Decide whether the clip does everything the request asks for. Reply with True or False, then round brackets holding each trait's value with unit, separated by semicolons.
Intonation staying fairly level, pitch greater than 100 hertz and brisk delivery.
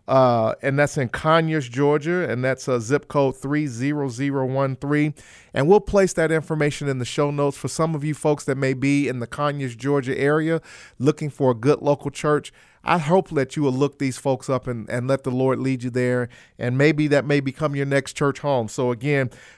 True (2.3 semitones; 140 Hz; 210 wpm)